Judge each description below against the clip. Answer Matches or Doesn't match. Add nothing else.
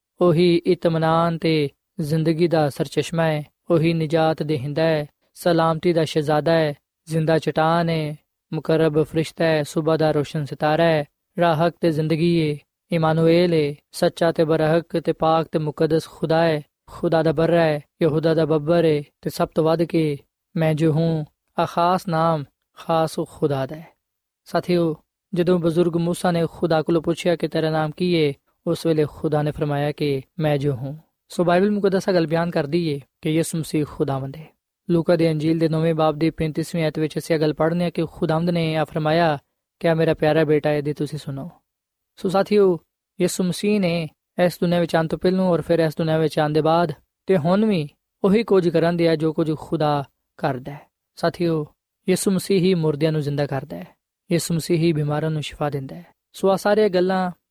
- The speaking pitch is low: Doesn't match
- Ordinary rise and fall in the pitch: Doesn't match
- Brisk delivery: Matches